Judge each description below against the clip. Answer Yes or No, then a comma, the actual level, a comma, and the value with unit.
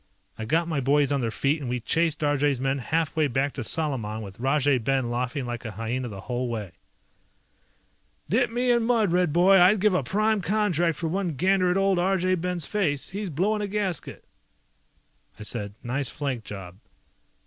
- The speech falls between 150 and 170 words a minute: No, average, 190 wpm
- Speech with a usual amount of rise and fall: No, wide, 6.8 semitones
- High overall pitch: No, medium, 150 Hz